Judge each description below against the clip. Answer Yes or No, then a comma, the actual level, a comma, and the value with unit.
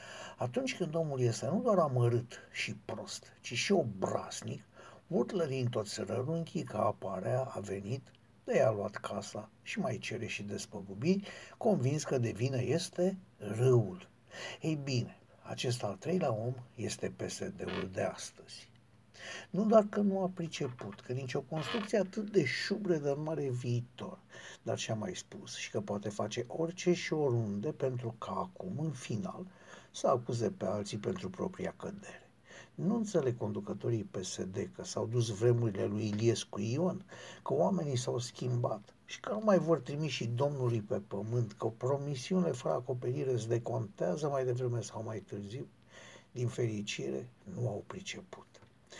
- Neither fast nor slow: Yes, average, 155 wpm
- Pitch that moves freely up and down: Yes, wide, 6.1 semitones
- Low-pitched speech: Yes, low, 125 Hz